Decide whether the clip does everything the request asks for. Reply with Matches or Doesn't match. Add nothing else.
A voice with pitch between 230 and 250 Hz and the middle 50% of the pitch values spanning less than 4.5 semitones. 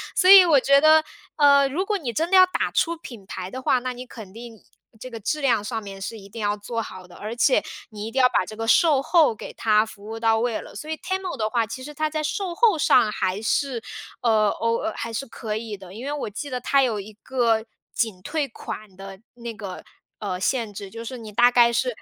Doesn't match